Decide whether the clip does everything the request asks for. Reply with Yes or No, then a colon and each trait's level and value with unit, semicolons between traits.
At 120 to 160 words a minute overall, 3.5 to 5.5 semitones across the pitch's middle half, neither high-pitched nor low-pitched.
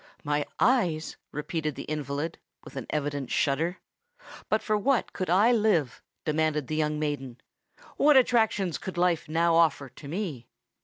Yes: average, 150 wpm; average, 4.4 semitones; medium, 160 Hz